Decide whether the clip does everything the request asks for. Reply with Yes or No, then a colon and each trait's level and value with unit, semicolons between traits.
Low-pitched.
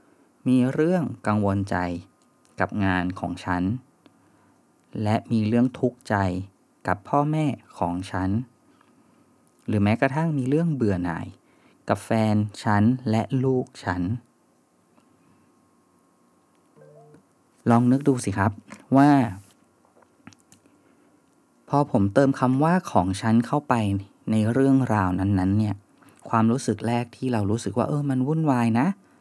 Yes: low, 115 Hz